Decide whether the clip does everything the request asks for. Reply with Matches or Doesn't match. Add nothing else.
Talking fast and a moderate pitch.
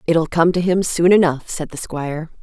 Matches